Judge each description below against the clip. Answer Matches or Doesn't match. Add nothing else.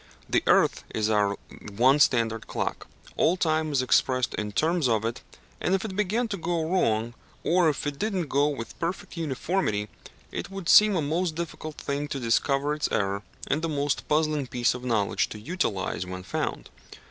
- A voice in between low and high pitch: Matches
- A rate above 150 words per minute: Matches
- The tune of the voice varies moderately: Doesn't match